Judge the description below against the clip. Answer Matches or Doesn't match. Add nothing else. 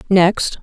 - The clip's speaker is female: Matches